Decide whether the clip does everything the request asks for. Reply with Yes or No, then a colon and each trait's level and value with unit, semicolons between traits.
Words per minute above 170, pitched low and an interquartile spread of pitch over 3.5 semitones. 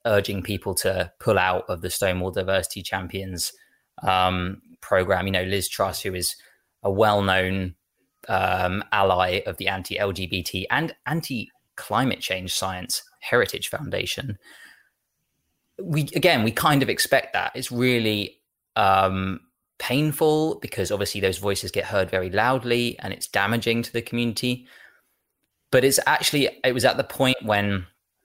No: average, 145 wpm; low, 100 Hz; average, 4.1 semitones